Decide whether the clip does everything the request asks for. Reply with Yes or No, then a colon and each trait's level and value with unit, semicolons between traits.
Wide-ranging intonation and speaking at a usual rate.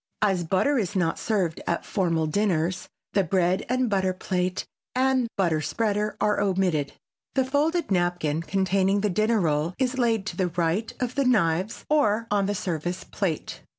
No: average, 3.8 semitones; average, 165 wpm